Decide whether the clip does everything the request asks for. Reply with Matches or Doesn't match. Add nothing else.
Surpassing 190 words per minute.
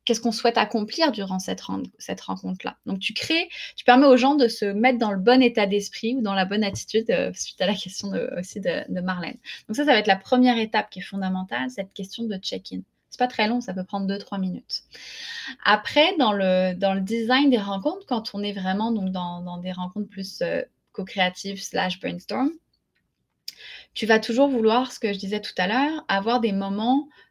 Matches